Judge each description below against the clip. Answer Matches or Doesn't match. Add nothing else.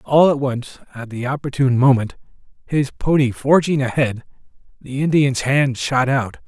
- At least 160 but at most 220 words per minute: Doesn't match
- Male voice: Matches